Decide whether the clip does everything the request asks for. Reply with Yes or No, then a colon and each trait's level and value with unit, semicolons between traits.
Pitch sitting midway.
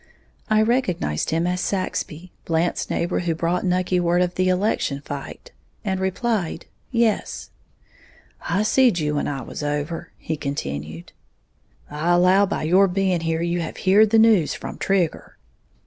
Yes: medium, 175 Hz